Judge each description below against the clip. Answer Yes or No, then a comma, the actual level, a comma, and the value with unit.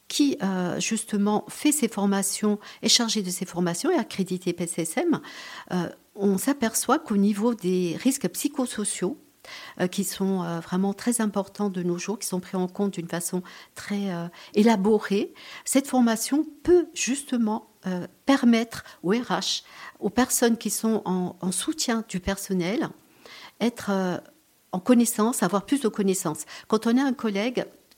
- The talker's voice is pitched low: No, high, 205 Hz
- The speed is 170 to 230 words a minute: No, average, 155 wpm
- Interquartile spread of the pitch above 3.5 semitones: Yes, average, 4.4 semitones